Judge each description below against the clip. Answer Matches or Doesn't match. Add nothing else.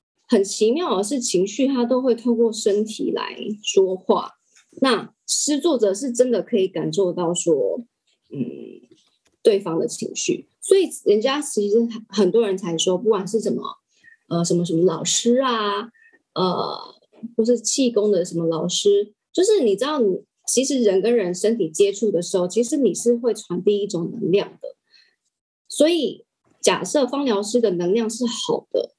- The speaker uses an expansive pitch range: Doesn't match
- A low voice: Doesn't match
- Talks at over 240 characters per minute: Doesn't match